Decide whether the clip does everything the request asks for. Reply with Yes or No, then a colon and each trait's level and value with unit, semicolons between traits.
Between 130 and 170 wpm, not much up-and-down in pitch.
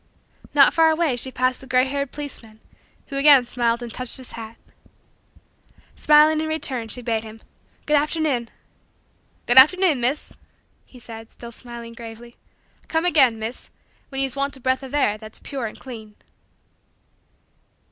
No: average, 155 wpm; average, 3.6 semitones